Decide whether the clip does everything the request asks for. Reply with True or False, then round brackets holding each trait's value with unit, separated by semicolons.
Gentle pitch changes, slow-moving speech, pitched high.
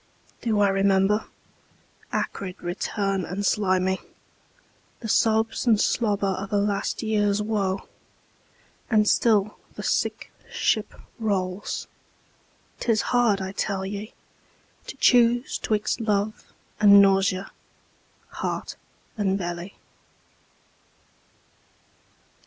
True (2.0 semitones; 95 wpm; 200 Hz)